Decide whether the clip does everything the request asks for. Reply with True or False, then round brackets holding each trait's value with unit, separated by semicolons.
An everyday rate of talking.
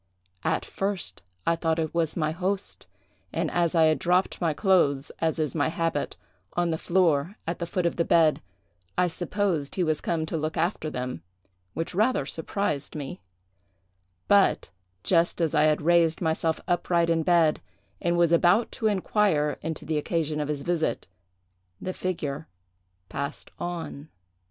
True (160 wpm)